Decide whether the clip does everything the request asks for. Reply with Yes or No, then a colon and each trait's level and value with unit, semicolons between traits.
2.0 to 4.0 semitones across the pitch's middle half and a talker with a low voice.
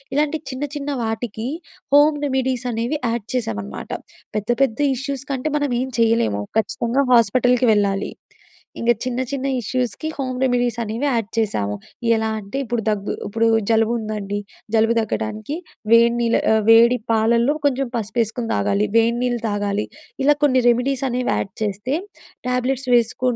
No: average, 2.9 semitones; high, 235 Hz